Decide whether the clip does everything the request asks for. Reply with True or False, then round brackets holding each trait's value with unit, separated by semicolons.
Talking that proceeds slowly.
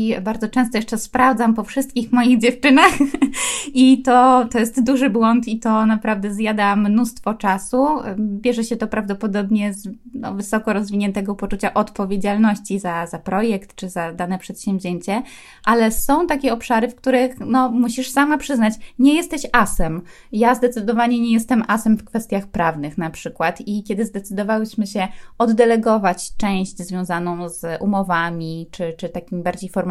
False (150 wpm)